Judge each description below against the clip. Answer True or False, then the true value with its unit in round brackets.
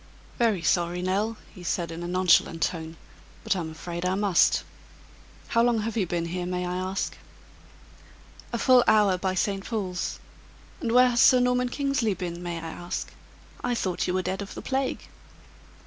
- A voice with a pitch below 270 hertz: True (185 Hz)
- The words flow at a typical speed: True (180 wpm)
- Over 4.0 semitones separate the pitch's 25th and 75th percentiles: True (4.6 semitones)